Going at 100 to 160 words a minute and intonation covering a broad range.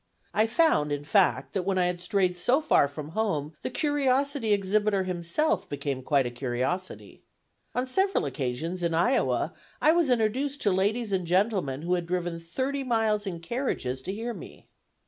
No: average, 170 wpm; wide, 6.3 semitones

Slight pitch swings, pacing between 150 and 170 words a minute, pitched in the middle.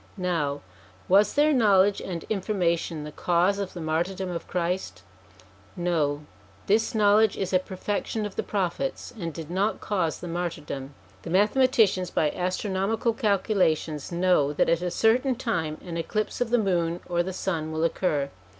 No: average, 3.7 semitones; average, 160 wpm; medium, 180 Hz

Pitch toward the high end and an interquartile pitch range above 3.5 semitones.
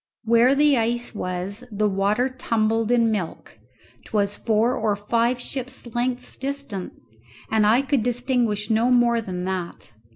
No: high, 230 Hz; average, 3.0 semitones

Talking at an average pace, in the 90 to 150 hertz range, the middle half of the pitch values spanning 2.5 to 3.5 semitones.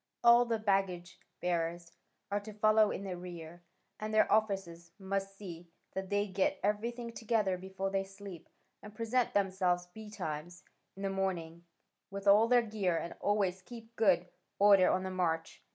No: average, 160 wpm; high, 195 Hz; average, 3.0 semitones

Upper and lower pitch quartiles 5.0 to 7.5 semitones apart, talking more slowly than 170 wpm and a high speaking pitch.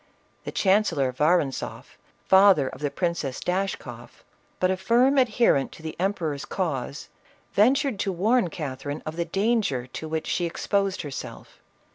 No: wide, 5.5 semitones; average, 150 wpm; medium, 175 Hz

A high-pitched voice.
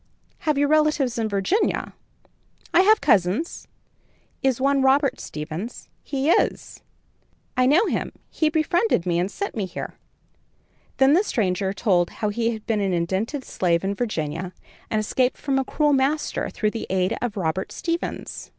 Yes: high, 235 Hz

